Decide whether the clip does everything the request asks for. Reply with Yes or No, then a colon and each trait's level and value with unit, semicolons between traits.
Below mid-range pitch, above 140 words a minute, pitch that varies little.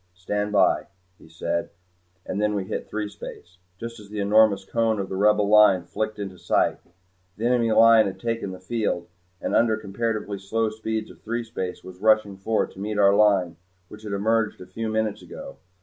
Yes: low, 105 Hz; average, 190 wpm; narrow, 2.3 semitones